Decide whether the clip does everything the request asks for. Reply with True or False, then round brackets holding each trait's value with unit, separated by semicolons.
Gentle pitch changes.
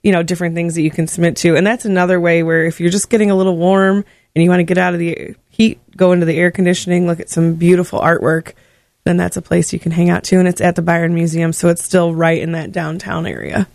True (1.5 semitones)